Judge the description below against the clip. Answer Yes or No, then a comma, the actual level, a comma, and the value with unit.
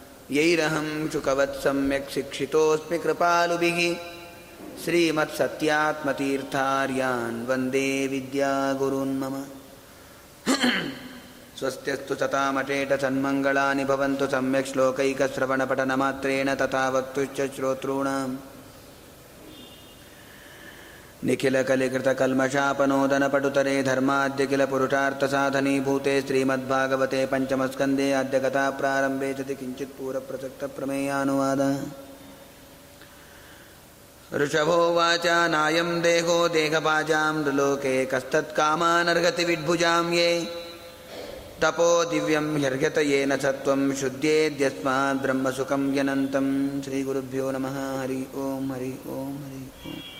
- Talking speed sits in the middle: No, slow, 60 wpm